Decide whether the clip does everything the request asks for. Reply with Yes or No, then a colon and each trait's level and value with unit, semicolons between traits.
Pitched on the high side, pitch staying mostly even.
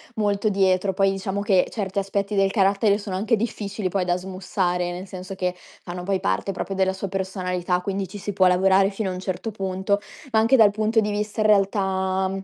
Yes: high, 195 Hz; narrow, 1.5 semitones